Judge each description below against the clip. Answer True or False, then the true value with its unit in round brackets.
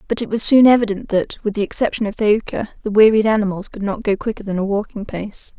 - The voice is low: False (210 Hz)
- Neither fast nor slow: False (235 wpm)